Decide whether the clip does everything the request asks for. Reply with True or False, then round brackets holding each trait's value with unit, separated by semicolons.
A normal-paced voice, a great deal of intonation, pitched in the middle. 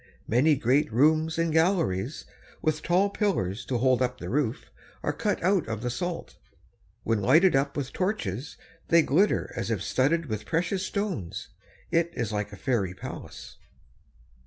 True (160 wpm; 6.5 semitones; 145 Hz)